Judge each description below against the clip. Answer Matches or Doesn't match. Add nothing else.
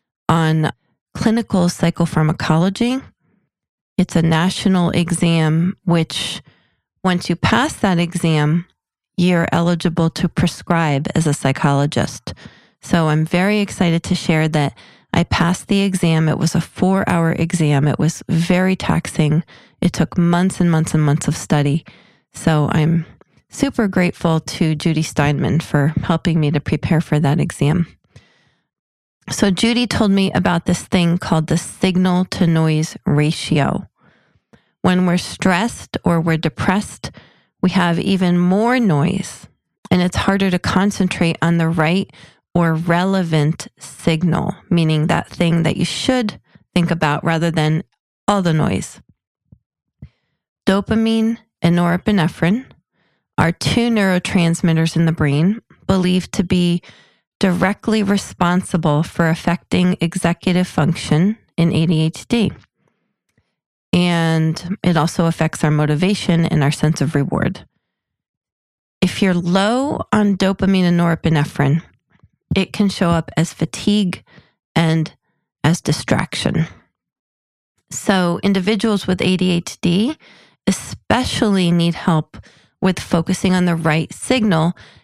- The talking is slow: Matches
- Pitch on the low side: Doesn't match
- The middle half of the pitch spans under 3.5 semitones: Matches